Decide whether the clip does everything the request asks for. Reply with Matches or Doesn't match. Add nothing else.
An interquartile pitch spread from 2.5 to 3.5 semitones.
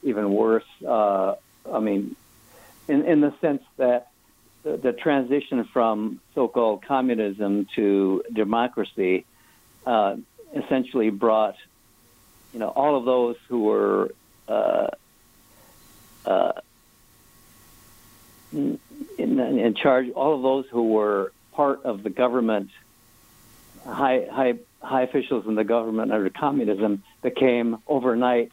Matches